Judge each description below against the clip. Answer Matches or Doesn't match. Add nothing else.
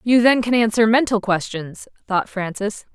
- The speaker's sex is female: Matches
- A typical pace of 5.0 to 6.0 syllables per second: Doesn't match